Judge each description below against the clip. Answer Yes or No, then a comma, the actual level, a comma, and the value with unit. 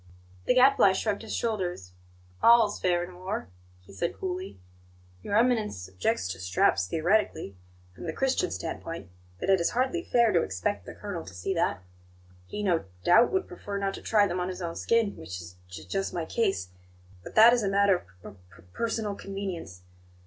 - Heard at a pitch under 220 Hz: Yes, high, 190 Hz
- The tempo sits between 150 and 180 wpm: No, average, 190 wpm